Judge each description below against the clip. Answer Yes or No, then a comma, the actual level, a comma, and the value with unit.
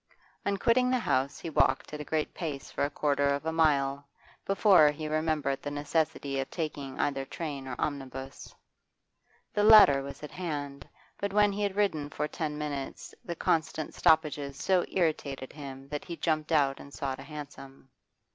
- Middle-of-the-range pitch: Yes, medium, 150 Hz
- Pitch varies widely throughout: No, average, 2.7 semitones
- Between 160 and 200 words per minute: Yes, average, 175 wpm